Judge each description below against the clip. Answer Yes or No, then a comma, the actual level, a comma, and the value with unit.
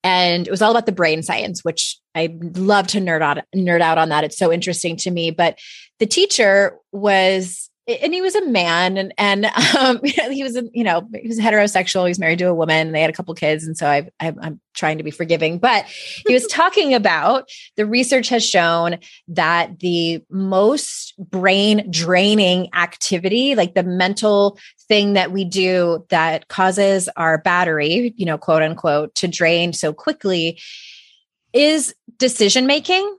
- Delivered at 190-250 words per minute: No, average, 180 wpm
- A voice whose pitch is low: No, medium, 185 Hz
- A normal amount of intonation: Yes, average, 4.2 semitones